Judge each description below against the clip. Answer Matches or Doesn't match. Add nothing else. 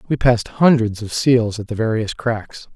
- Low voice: Matches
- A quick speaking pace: Doesn't match